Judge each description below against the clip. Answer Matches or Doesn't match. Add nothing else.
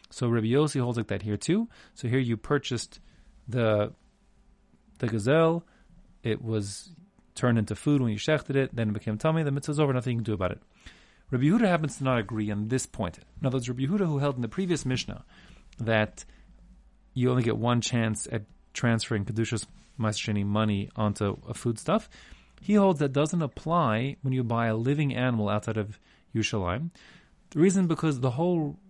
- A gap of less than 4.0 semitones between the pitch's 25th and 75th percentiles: Doesn't match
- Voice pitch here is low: Matches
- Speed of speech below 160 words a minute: Doesn't match